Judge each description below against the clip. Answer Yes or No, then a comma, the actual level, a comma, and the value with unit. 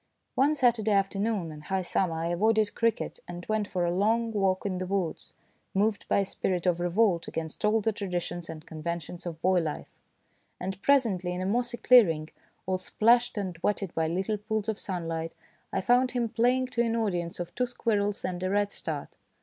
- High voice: Yes, high, 195 Hz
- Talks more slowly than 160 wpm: No, average, 190 wpm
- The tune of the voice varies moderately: Yes, average, 4.1 semitones